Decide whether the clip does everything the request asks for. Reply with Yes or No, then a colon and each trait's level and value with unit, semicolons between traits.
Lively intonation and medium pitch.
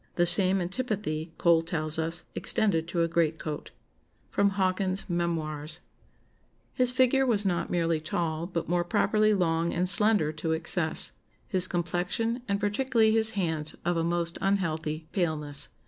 No: average, 3.6 semitones; medium, 175 Hz